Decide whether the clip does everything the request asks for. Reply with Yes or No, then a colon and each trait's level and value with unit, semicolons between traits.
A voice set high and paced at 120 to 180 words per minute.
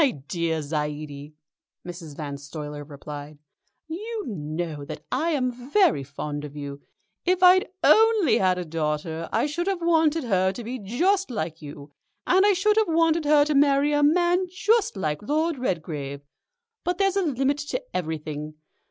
Yes: high, 230 Hz; average, 165 wpm